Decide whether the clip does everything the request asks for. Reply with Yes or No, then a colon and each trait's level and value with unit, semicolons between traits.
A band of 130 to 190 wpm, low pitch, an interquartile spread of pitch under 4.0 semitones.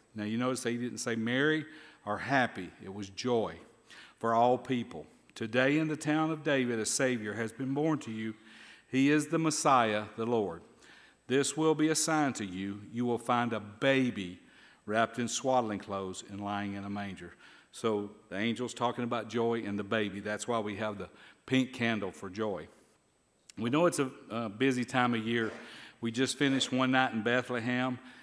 Yes: average, 185 wpm; low, 120 Hz; average, 3.6 semitones